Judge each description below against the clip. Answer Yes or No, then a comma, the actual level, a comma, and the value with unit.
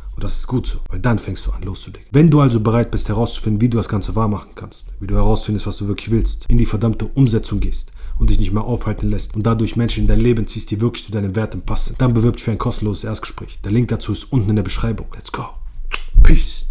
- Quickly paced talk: Yes, fast, 260 wpm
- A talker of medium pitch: No, low, 110 Hz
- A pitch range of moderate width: No, narrow, 2.1 semitones